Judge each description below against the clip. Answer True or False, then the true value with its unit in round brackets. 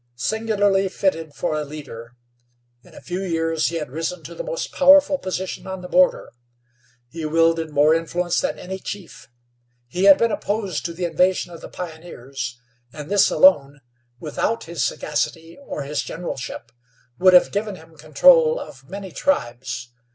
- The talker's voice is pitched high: False (170 Hz)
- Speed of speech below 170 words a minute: True (160 wpm)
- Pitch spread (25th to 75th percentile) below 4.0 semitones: False (4.5 semitones)